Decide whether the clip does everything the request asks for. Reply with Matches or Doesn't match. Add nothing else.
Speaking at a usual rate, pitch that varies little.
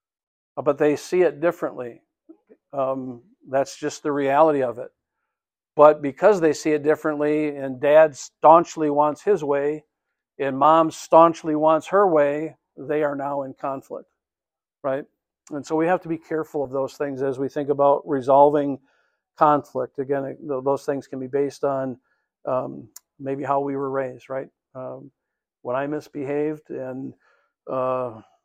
Matches